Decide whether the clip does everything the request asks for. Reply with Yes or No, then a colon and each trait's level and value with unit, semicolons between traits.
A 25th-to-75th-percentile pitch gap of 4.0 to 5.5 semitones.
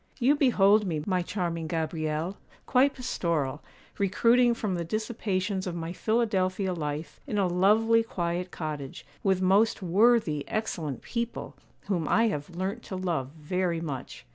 Yes: average, 4.7 semitones